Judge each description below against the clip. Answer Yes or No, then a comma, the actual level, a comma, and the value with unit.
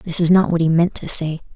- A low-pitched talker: No, medium, 170 Hz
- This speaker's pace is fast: Yes, fast, 310 wpm